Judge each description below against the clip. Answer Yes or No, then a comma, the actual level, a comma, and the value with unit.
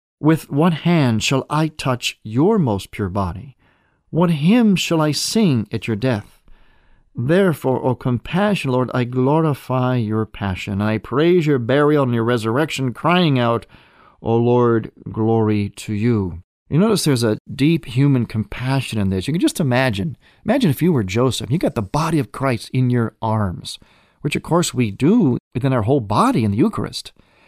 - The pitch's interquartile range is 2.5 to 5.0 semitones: No, wide, 5.6 semitones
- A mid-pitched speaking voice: No, low, 130 Hz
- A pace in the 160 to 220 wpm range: Yes, average, 170 wpm